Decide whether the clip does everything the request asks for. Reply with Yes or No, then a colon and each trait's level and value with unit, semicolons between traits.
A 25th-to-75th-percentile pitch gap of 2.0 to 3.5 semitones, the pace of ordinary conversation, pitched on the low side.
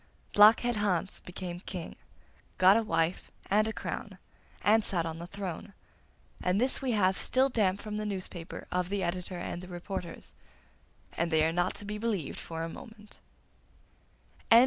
No: average, 3.2 semitones; average, 165 wpm; high, 190 Hz